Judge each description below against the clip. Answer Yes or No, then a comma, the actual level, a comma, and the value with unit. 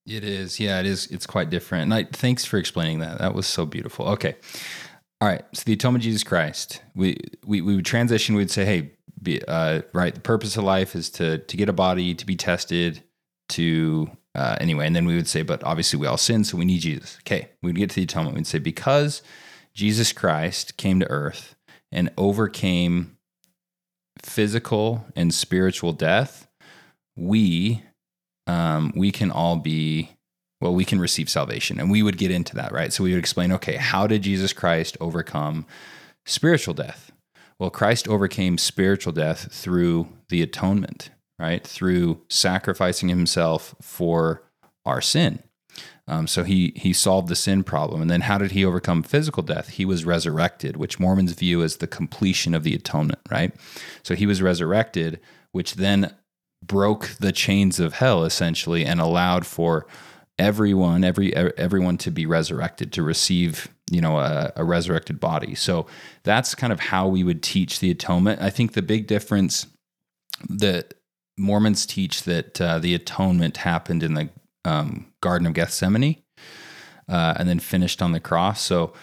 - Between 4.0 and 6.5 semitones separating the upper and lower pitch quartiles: No, average, 3.3 semitones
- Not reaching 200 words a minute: Yes, average, 175 wpm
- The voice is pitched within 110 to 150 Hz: No, very low, 90 Hz